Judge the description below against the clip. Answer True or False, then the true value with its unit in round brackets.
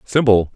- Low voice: True (110 Hz)